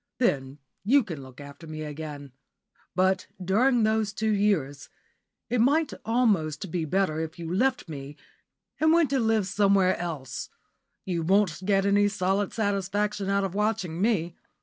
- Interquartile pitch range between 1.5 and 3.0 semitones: No, average, 5.0 semitones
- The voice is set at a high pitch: Yes, high, 195 Hz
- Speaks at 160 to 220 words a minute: No, average, 150 wpm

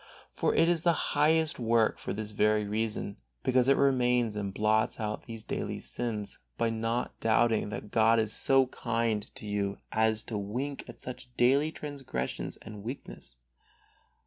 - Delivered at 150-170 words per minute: Yes, average, 160 wpm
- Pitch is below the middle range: Yes, low, 115 Hz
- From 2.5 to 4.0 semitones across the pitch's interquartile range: Yes, average, 3.1 semitones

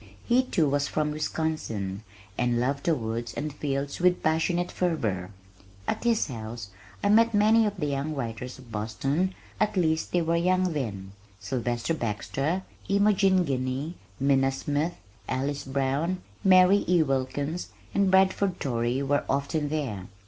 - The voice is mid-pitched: Yes, medium, 145 Hz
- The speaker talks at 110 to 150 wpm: Yes, average, 145 wpm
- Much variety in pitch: Yes, wide, 5.8 semitones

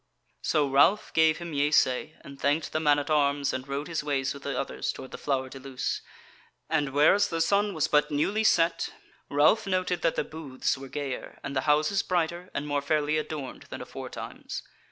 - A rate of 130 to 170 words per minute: No, average, 195 wpm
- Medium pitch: Yes, medium, 150 Hz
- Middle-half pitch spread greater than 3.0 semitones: No, average, 2.7 semitones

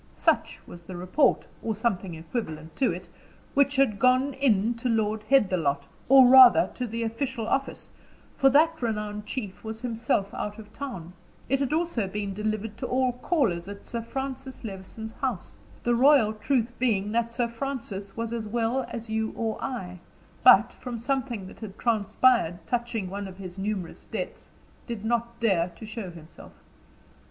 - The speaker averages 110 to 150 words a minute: No, average, 165 wpm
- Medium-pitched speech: No, high, 225 Hz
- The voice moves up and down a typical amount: Yes, average, 3.9 semitones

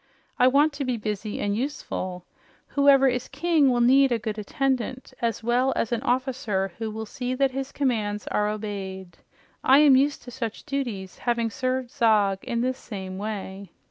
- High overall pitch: Yes, high, 240 Hz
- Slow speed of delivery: No, average, 175 wpm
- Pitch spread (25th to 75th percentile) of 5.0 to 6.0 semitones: No, average, 4.1 semitones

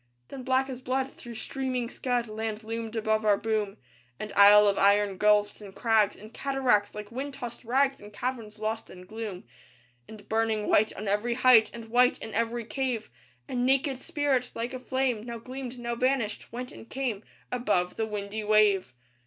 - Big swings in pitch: No, average, 3.2 semitones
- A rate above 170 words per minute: Yes, average, 180 wpm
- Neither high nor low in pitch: No, high, 225 Hz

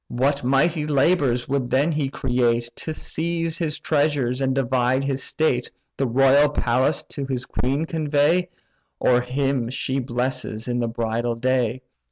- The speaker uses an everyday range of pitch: Yes, average, 3.1 semitones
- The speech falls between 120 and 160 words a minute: Yes, average, 150 wpm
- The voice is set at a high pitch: No, low, 135 Hz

